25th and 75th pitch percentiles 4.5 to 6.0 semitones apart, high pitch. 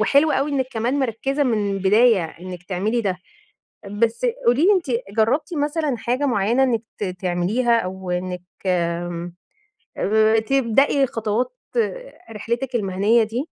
Yes: wide, 5.5 semitones; high, 225 Hz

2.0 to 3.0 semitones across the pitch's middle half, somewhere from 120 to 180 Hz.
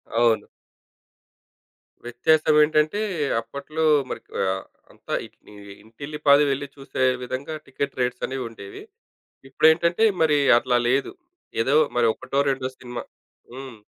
No: average, 3.6 semitones; low, 135 Hz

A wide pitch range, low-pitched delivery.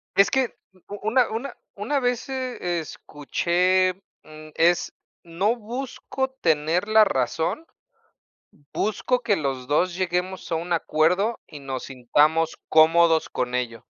No: wide, 5.8 semitones; medium, 175 Hz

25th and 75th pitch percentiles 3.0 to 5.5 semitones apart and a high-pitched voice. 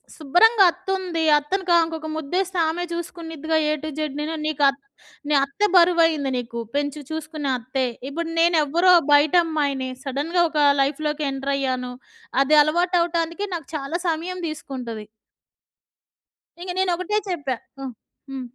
Yes: average, 3.7 semitones; very high, 315 Hz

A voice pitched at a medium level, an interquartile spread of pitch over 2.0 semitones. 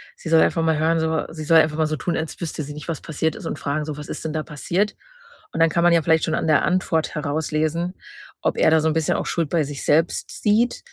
No: medium, 160 Hz; narrow, 1.4 semitones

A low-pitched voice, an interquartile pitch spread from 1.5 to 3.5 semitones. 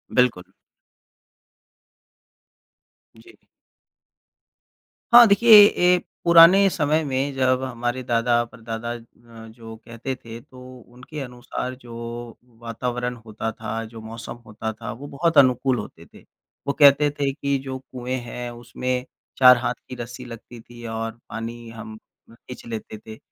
Yes: low, 120 Hz; narrow, 2.5 semitones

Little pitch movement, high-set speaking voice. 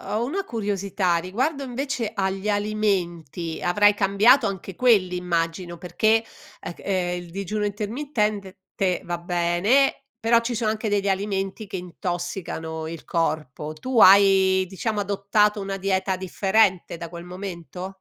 No: average, 3.1 semitones; high, 195 Hz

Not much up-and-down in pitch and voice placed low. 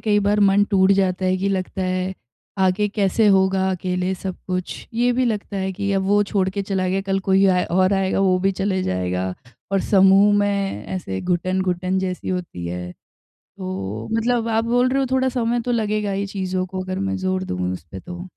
No: narrow, 1.8 semitones; high, 190 Hz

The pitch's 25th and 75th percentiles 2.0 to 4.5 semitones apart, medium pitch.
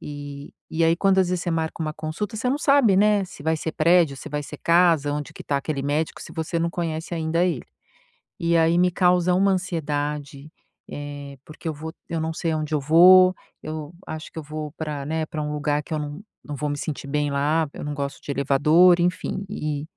Yes: average, 2.8 semitones; medium, 155 Hz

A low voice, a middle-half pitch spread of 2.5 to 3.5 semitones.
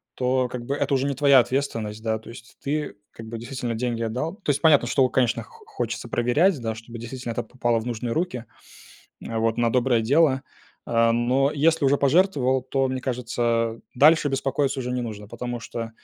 Yes: low, 125 Hz; average, 3.2 semitones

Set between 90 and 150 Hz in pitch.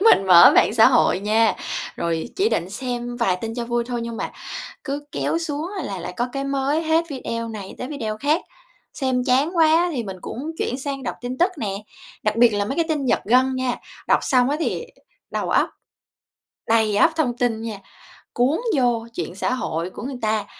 No: high, 245 Hz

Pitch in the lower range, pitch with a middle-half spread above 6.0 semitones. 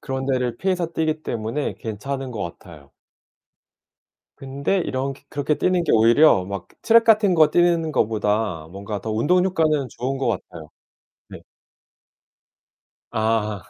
Yes: low, 130 Hz; wide, 6.6 semitones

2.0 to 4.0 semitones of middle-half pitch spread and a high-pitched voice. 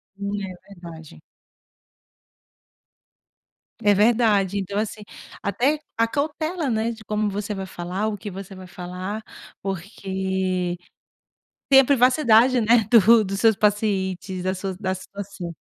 Yes: average, 2.9 semitones; high, 200 Hz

